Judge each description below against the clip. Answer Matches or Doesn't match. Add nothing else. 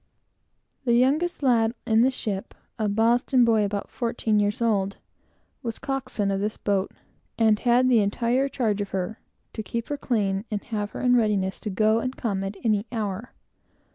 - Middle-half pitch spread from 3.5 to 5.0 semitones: Doesn't match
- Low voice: Doesn't match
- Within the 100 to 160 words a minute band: Doesn't match